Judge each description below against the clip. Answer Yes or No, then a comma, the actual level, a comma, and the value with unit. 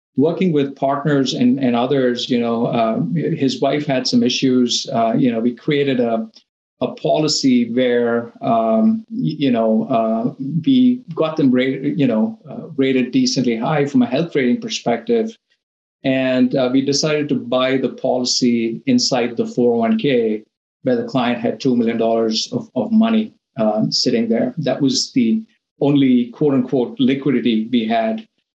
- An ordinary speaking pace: Yes, average, 160 wpm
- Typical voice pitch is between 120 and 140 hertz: Yes, low, 135 Hz